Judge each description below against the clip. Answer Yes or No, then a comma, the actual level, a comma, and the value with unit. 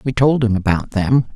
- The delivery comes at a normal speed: No, fast, 220 wpm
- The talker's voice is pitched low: Yes, low, 115 Hz